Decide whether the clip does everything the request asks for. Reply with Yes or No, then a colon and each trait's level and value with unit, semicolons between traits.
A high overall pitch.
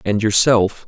No: low, 105 Hz